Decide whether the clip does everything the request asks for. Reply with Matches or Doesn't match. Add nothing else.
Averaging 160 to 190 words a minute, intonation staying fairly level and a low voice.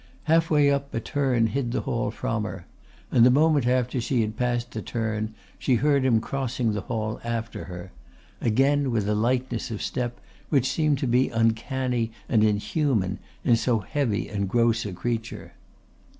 Doesn't match